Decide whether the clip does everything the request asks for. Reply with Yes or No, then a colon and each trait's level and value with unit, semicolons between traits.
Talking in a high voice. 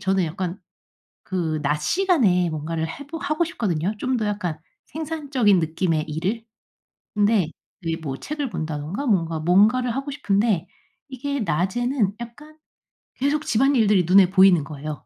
Yes: high, 200 Hz